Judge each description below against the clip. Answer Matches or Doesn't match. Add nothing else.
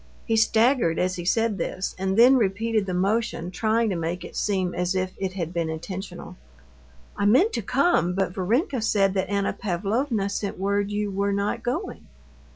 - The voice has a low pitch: Doesn't match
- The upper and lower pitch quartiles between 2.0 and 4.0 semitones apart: Matches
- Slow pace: Doesn't match